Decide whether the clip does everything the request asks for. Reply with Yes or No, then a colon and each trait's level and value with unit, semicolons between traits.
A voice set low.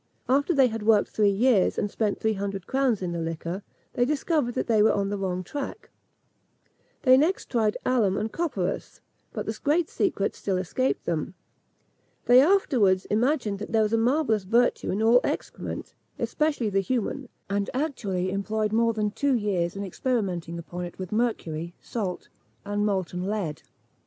No: high, 215 Hz